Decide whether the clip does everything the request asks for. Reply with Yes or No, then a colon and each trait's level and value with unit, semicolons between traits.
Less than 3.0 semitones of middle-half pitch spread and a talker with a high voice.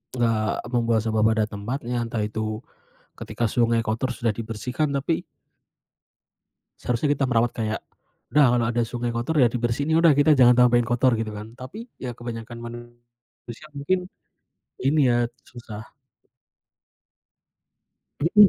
No: narrow, 2.4 semitones; low, 120 Hz